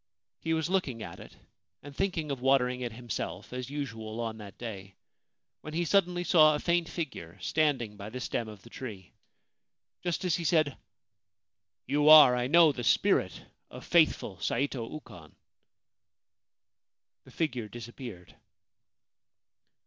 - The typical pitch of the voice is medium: No, low, 130 Hz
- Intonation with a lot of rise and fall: Yes, wide, 5.8 semitones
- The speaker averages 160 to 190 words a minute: No, average, 150 wpm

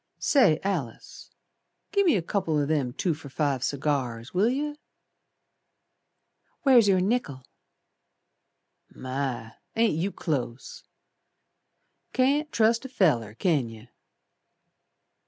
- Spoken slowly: Yes, slow, 105 wpm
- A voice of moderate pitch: Yes, medium, 160 Hz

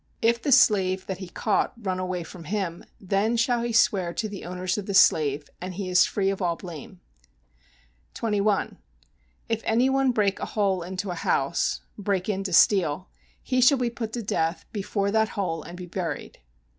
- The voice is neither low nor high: No, high, 195 Hz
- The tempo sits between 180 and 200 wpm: Yes, average, 190 wpm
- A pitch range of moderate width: Yes, average, 3.3 semitones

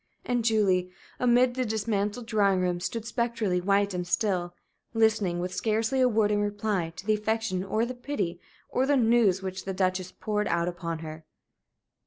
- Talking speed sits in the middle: Yes, average, 175 wpm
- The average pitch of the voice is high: Yes, high, 205 Hz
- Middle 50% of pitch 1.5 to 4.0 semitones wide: Yes, average, 3.7 semitones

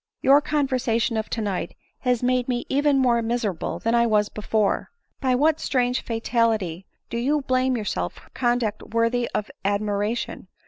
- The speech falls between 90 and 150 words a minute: No, average, 165 wpm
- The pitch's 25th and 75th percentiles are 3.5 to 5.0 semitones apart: No, average, 3.0 semitones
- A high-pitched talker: Yes, high, 235 Hz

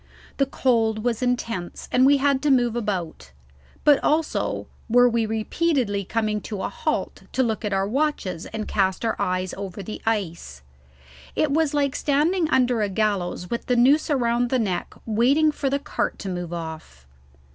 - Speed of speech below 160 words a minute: No, average, 175 wpm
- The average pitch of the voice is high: Yes, high, 230 Hz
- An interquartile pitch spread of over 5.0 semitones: Yes, wide, 5.6 semitones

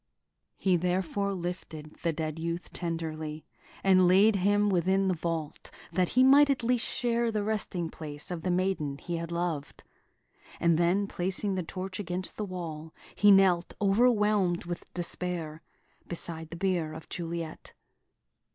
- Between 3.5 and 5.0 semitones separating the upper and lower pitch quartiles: No, average, 3.0 semitones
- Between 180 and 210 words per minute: No, average, 150 wpm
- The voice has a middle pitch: Yes, medium, 180 Hz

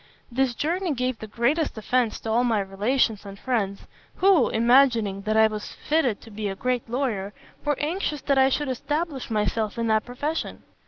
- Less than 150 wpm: No, average, 180 wpm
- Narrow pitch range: No, average, 4.3 semitones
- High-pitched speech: Yes, high, 240 Hz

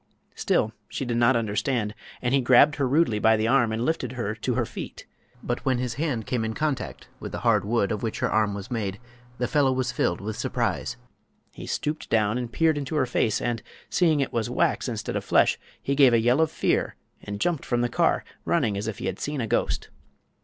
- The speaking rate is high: Yes, fast, 225 wpm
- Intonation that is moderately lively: Yes, average, 3.6 semitones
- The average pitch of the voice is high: No, low, 120 Hz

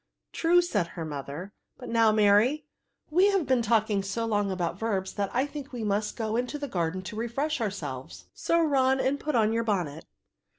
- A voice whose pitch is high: Yes, high, 220 Hz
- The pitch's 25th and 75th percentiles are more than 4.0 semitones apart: Yes, wide, 5.6 semitones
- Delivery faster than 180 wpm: Yes, average, 200 wpm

